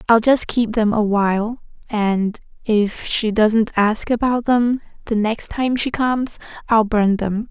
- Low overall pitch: No, high, 220 Hz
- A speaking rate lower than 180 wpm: Yes, average, 160 wpm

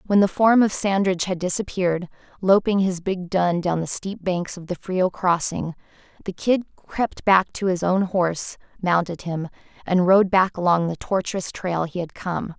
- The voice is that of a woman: Yes, female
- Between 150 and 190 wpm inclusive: Yes, average, 185 wpm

